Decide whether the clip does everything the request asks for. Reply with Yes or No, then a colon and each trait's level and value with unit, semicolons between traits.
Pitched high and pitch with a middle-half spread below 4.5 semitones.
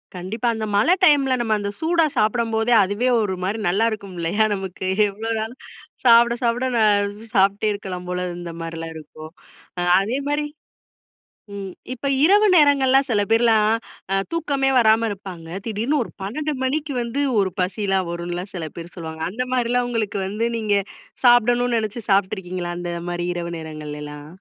No: high, 215 Hz; average, 5.0 semitones